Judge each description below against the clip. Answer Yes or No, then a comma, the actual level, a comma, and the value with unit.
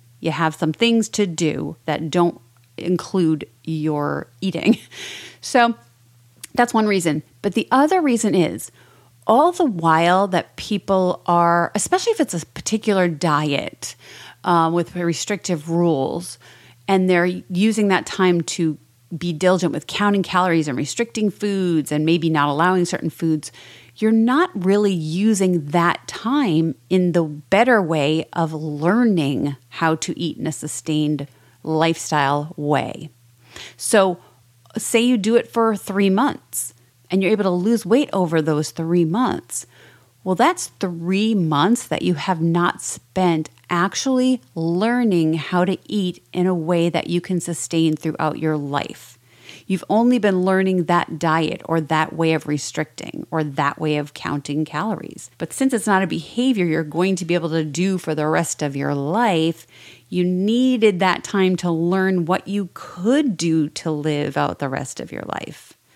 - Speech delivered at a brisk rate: No, average, 155 wpm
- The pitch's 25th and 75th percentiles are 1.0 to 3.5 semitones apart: No, average, 4.1 semitones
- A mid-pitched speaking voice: Yes, medium, 170 Hz